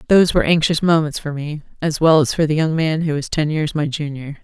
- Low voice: No, medium, 155 Hz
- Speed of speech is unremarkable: No, fast, 255 wpm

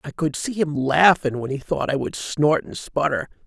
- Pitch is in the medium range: Yes, medium, 150 Hz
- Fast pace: Yes, fast, 225 wpm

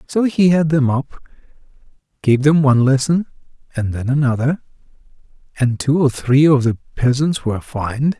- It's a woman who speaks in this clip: No, male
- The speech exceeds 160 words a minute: No, average, 155 wpm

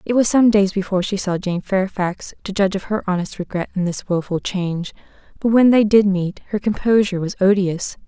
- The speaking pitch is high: Yes, high, 195 Hz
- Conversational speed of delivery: No, fast, 210 wpm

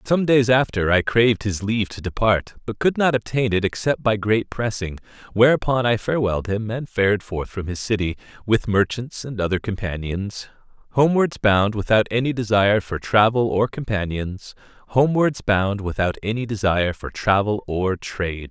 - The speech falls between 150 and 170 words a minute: Yes, average, 165 wpm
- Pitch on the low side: Yes, low, 105 Hz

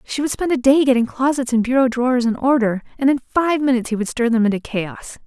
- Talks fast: Yes, fast, 250 wpm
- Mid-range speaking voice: No, very high, 250 Hz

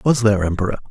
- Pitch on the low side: Yes, low, 110 Hz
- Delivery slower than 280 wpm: Yes, average, 200 wpm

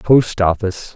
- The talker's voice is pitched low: Yes, low, 100 Hz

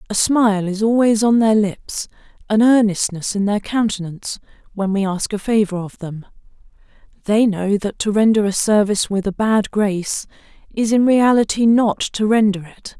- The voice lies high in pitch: Yes, high, 210 Hz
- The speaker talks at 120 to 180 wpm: Yes, average, 170 wpm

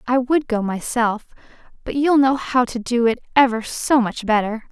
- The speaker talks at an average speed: Yes, average, 190 wpm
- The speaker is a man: No, female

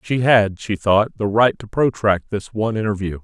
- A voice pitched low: Yes, low, 105 Hz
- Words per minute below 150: No, fast, 205 wpm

